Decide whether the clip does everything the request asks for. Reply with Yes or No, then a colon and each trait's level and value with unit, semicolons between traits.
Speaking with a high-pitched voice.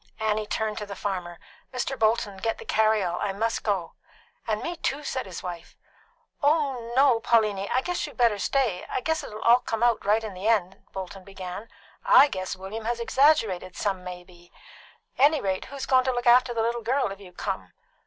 Yes: high, 220 Hz